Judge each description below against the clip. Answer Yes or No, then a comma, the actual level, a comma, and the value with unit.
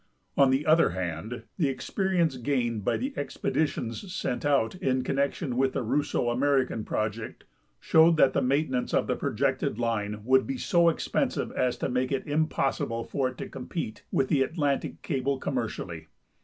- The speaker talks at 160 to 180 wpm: Yes, average, 170 wpm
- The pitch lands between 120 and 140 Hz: Yes, low, 135 Hz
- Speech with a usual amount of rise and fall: Yes, average, 3.9 semitones